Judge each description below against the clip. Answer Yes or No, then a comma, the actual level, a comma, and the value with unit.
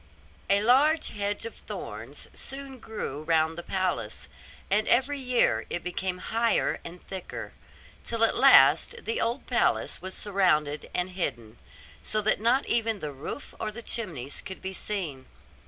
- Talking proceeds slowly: No, average, 155 wpm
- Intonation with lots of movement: Yes, wide, 6.3 semitones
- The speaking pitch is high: Yes, high, 195 Hz